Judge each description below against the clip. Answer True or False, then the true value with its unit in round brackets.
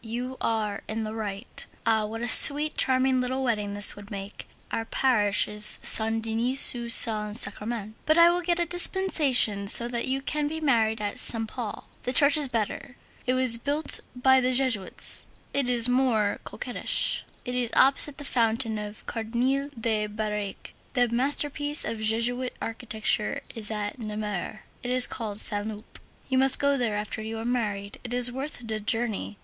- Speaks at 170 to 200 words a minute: True (175 wpm)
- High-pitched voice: True (235 Hz)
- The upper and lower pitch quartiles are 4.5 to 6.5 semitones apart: False (3.3 semitones)